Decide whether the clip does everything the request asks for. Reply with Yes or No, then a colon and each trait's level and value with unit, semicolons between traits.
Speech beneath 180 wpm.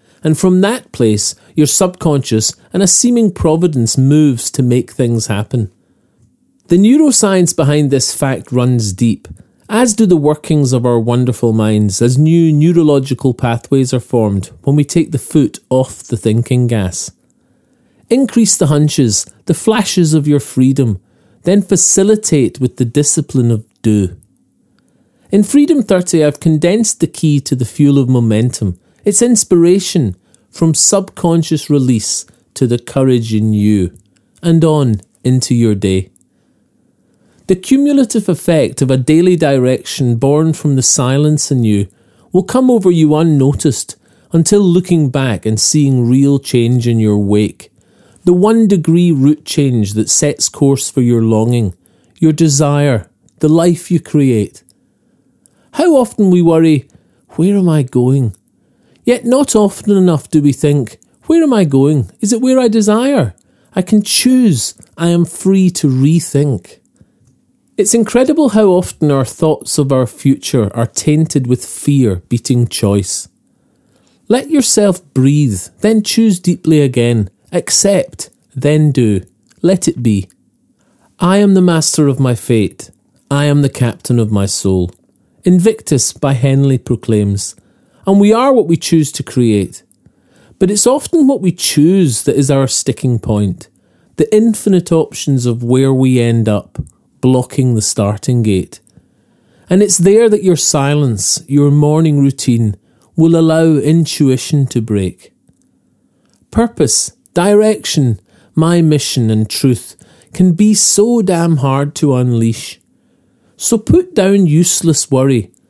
Yes: average, 140 wpm